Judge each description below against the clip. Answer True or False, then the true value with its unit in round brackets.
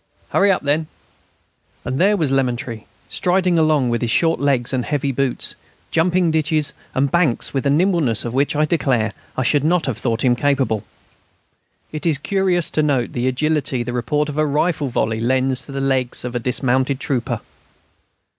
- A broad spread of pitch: False (3.7 semitones)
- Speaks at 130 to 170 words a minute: False (180 wpm)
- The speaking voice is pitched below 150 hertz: True (140 Hz)